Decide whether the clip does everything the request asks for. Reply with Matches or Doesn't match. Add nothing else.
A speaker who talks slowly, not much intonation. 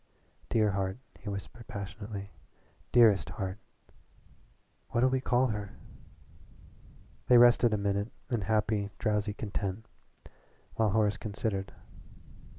Matches